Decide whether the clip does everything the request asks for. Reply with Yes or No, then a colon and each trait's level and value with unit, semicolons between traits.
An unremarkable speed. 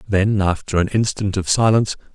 Yes: average, 170 wpm